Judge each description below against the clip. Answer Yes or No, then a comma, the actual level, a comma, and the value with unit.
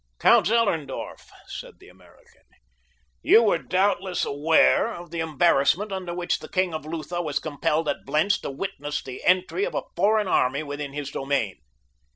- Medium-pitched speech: Yes, medium, 165 Hz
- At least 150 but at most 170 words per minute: Yes, average, 165 wpm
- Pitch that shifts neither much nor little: Yes, average, 4.6 semitones